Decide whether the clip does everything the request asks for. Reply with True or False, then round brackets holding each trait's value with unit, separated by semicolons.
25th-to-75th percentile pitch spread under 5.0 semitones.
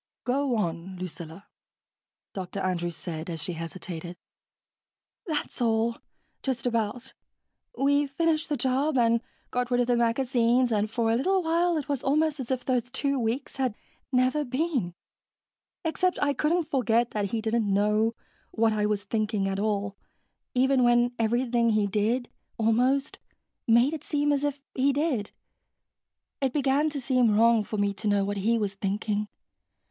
True (4.5 semitones)